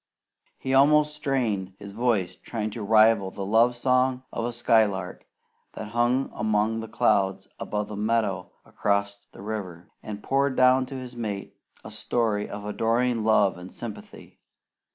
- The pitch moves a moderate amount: Yes, average, 3.3 semitones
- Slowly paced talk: No, average, 155 wpm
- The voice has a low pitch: Yes, low, 110 Hz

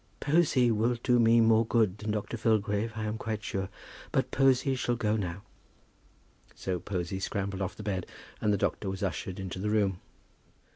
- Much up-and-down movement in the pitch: No, average, 3.0 semitones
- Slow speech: No, average, 180 wpm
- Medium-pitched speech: No, low, 105 Hz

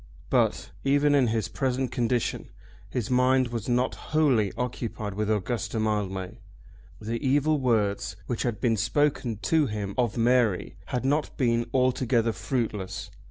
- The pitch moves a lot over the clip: No, average, 3.2 semitones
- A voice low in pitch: Yes, low, 120 Hz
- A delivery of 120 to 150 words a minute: Yes, average, 140 wpm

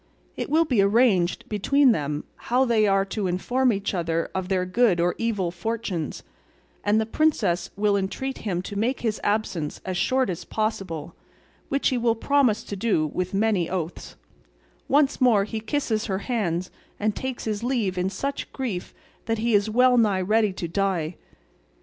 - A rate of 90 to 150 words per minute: No, average, 175 wpm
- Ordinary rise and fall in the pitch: Yes, average, 4.3 semitones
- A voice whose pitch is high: Yes, high, 210 Hz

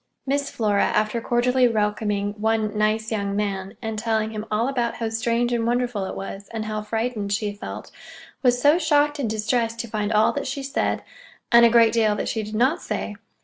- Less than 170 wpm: No, average, 200 wpm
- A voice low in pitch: No, high, 225 Hz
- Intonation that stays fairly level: Yes, narrow, 2.3 semitones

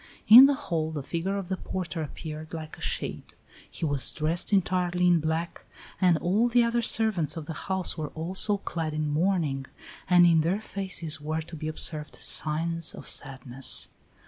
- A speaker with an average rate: Yes, average, 175 wpm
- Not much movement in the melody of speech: No, average, 3.3 semitones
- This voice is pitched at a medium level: Yes, medium, 165 Hz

